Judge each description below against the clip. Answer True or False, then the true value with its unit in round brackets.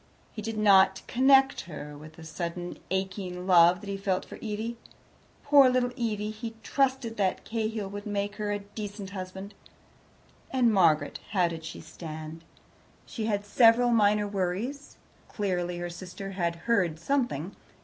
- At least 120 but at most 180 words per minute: True (150 wpm)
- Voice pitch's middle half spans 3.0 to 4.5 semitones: True (4.1 semitones)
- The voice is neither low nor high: False (200 Hz)